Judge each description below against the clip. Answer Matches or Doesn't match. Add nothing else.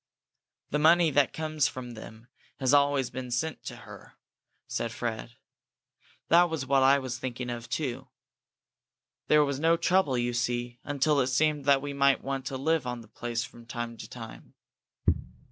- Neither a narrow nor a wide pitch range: Matches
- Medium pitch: Doesn't match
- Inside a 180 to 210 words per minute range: Doesn't match